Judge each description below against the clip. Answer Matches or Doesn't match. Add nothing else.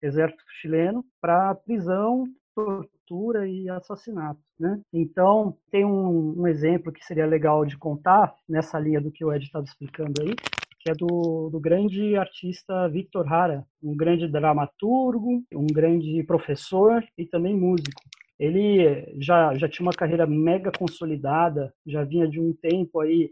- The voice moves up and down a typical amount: Matches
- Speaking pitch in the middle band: Matches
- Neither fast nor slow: Matches